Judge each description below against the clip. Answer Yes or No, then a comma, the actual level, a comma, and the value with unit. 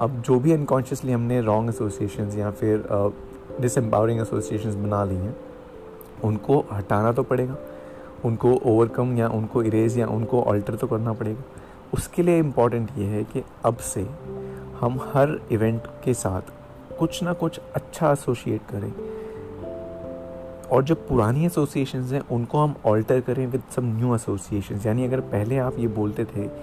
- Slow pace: No, average, 155 wpm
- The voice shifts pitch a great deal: No, average, 3.6 semitones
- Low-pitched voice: Yes, low, 115 Hz